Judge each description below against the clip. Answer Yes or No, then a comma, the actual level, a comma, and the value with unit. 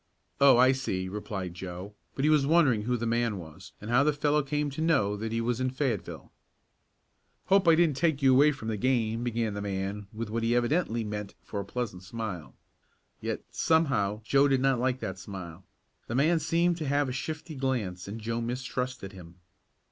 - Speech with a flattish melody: No, average, 5.1 semitones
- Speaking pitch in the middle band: No, low, 120 Hz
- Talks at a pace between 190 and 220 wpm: Yes, average, 200 wpm